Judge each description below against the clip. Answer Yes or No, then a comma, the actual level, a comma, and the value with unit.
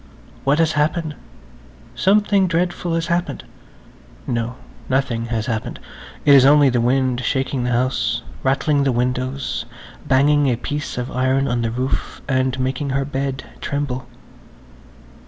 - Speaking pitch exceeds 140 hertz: No, low, 135 Hz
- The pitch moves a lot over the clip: No, average, 2.8 semitones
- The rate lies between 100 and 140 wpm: Yes, slow, 135 wpm